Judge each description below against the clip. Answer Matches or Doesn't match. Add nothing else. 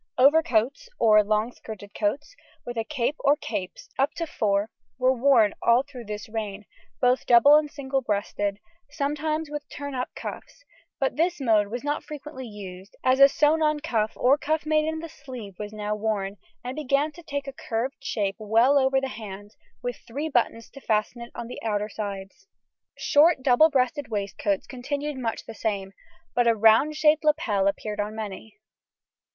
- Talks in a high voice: Matches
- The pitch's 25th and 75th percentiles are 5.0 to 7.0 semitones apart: Matches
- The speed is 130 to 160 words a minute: Doesn't match